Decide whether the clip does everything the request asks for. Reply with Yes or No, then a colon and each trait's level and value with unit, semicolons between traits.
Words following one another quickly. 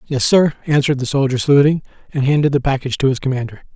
Yes: fast, 210 wpm